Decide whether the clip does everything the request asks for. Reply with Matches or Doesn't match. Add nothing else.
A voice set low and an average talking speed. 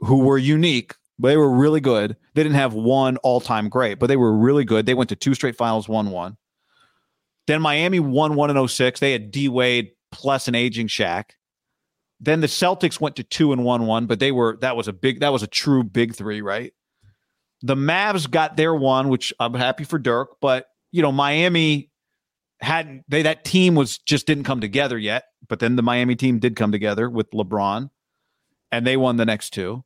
Doesn't match